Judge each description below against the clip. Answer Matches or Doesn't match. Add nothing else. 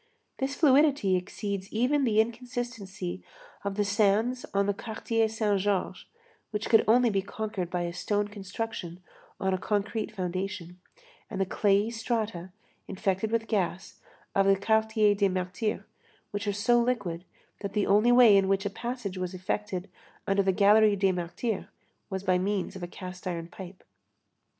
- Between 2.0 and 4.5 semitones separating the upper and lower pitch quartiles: Matches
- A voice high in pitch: Matches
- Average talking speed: Matches